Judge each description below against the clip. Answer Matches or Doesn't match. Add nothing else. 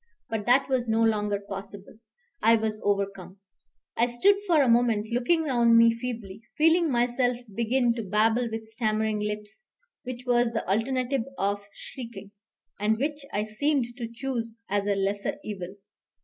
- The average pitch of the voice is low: Doesn't match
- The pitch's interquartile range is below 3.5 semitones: Matches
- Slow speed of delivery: Doesn't match